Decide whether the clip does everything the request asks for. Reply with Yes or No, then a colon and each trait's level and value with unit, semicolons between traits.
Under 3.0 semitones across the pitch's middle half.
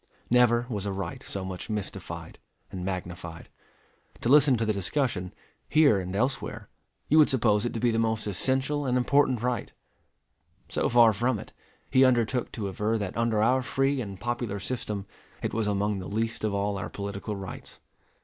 No: average, 3.8 semitones